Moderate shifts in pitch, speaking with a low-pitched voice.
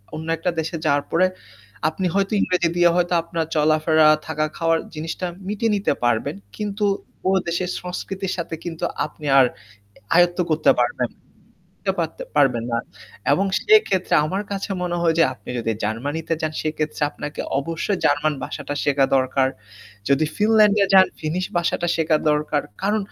No: average, 3.4 semitones; medium, 165 Hz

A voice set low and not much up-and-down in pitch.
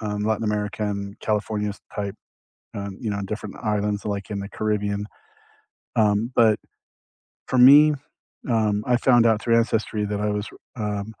Yes: low, 105 Hz; narrow, 1.4 semitones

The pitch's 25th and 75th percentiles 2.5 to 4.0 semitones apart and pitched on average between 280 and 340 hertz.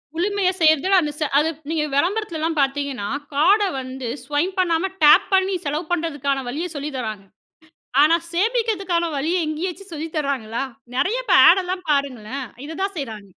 No: average, 4.9 semitones; very high, 320 Hz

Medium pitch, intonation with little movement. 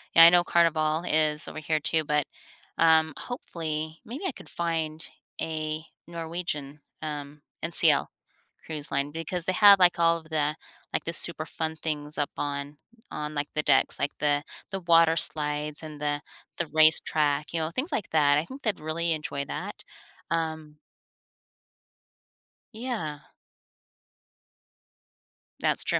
Yes: medium, 155 Hz; narrow, 1.9 semitones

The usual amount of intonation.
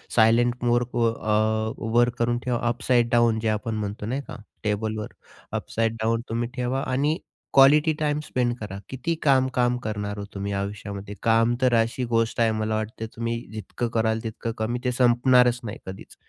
No: narrow, 2.0 semitones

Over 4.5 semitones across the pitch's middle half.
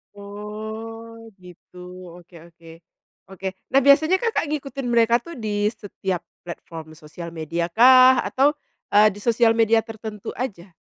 Yes: average, 4.9 semitones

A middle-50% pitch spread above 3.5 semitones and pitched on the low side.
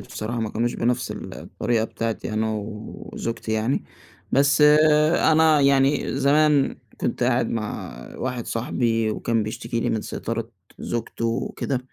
No: average, 3.2 semitones; low, 120 Hz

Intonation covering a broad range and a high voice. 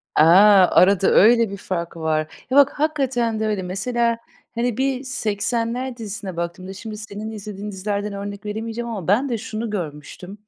No: average, 3.4 semitones; high, 210 Hz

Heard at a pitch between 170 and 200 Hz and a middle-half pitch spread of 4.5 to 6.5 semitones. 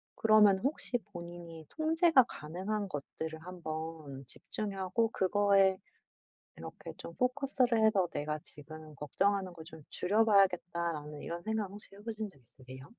Yes: medium, 185 Hz; average, 5.2 semitones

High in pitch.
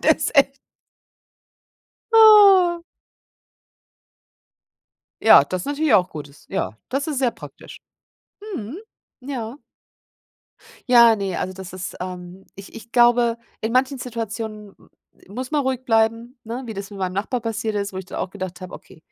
Yes: high, 225 Hz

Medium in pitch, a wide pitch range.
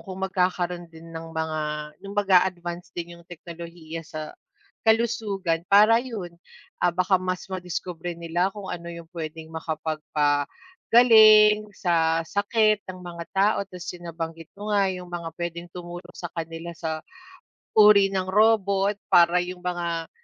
No: medium, 175 Hz; average, 3.1 semitones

